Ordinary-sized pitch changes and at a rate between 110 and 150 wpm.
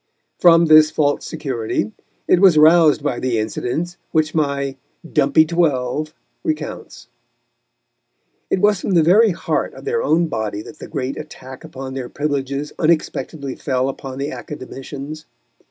Yes: average, 3.6 semitones; average, 140 wpm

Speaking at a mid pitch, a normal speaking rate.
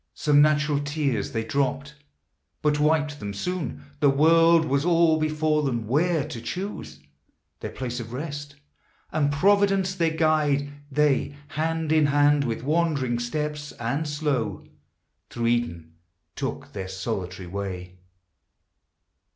No: medium, 145 Hz; slow, 125 wpm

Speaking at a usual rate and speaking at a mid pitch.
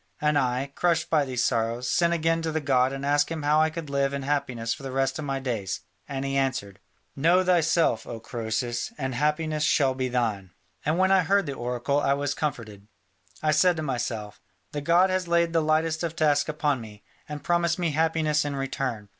No: fast, 210 wpm; medium, 145 Hz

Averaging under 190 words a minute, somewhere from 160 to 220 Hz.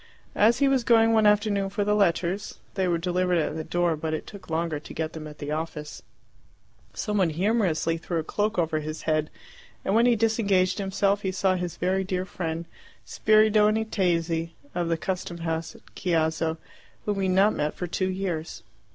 No: average, 195 wpm; medium, 185 Hz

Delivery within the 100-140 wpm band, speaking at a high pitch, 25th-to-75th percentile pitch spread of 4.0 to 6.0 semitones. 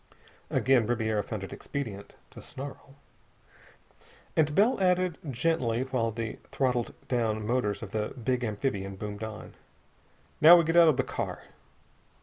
No: slow, 135 wpm; low, 120 Hz; average, 4.7 semitones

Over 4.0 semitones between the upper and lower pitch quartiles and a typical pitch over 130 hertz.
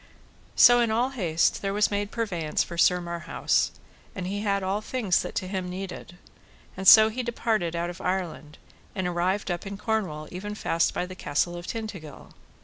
No: average, 3.3 semitones; high, 190 Hz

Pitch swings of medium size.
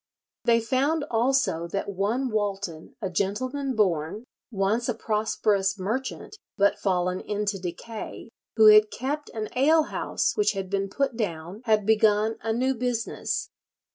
Yes: average, 4.0 semitones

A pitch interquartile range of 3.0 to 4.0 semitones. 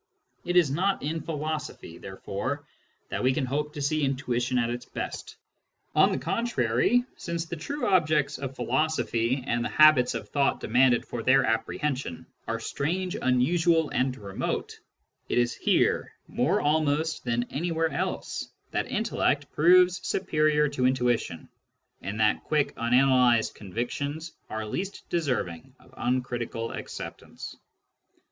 No: average, 4.6 semitones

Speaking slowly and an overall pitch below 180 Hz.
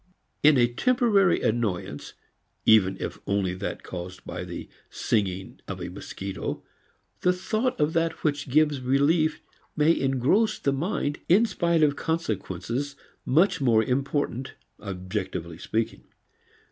Yes: slow, 125 wpm; low, 135 Hz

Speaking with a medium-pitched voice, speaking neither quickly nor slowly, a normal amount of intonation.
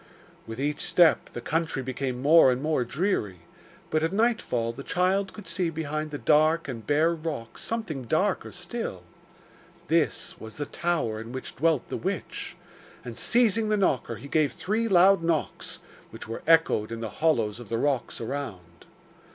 No: medium, 155 Hz; average, 165 wpm; wide, 5.9 semitones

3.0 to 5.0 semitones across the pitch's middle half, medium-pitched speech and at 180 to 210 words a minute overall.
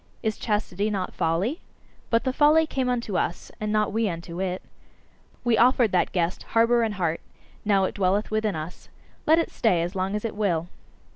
No: average, 4.1 semitones; high, 210 Hz; average, 190 wpm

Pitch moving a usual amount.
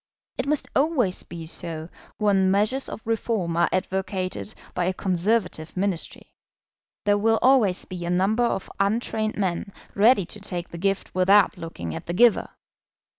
Yes: average, 3.4 semitones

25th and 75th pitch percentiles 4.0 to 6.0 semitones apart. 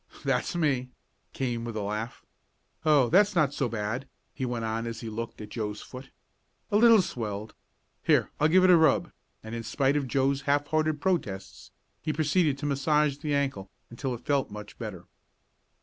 Yes: average, 4.9 semitones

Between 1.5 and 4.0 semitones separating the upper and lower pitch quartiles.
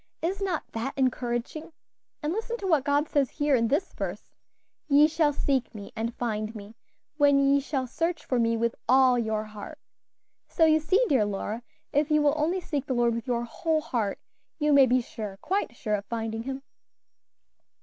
No: average, 4.8 semitones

